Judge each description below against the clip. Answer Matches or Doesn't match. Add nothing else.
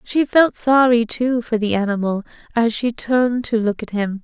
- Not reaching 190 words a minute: Doesn't match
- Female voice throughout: Matches